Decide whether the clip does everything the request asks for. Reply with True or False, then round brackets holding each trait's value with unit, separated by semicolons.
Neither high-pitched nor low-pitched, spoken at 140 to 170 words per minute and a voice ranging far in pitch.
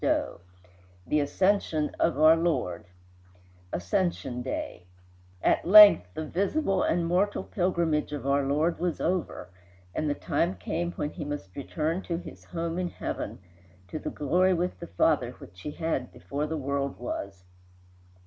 False (155 Hz; 150 wpm; 4.0 semitones)